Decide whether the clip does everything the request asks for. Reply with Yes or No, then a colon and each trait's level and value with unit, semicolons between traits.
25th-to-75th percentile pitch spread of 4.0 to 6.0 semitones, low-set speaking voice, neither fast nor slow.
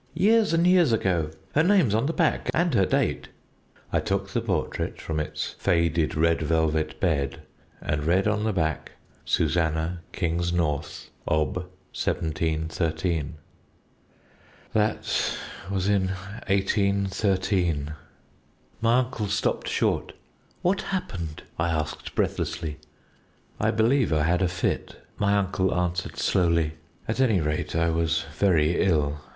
No: average, 4.5 semitones; very low, 90 Hz; slow, 125 wpm